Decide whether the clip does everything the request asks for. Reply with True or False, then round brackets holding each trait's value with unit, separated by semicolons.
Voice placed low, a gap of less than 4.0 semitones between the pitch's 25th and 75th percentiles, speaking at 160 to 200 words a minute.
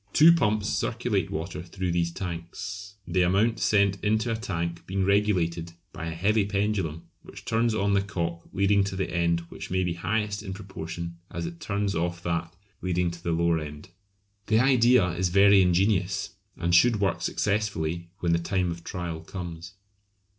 True (95 Hz; 3.3 semitones; 175 wpm)